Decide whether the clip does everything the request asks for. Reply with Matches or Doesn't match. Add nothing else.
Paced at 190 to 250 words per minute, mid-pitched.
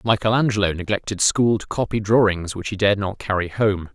Doesn't match